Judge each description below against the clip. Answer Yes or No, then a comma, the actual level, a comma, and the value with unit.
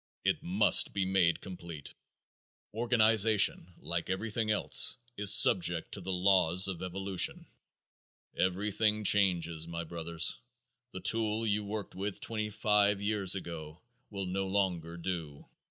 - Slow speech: Yes, slow, 125 wpm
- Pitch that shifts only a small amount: No, average, 3.3 semitones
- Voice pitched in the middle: No, very low, 95 Hz